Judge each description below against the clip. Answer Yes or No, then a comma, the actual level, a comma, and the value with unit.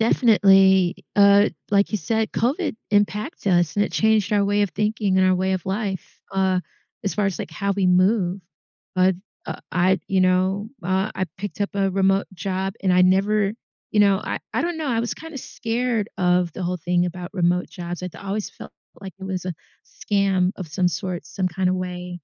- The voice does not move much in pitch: Yes, narrow, 2.0 semitones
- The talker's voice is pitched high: Yes, high, 195 Hz